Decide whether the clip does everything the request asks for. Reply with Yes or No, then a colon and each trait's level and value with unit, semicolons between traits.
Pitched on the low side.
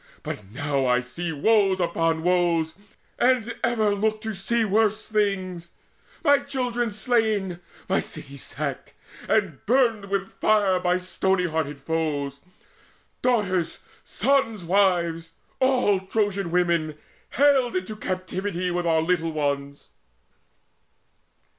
No: medium, 185 Hz